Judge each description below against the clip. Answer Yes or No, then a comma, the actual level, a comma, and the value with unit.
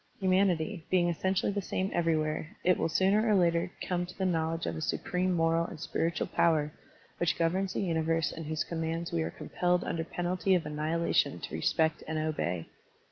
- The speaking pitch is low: No, medium, 170 Hz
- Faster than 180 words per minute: Yes, average, 190 wpm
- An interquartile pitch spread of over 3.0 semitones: No, narrow, 2.4 semitones